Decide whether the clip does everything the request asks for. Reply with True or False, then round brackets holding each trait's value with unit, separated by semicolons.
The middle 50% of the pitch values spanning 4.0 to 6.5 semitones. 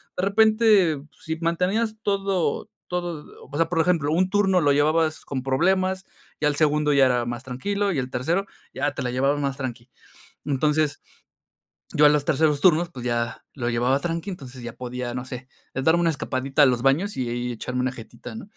True (5.4 semitones)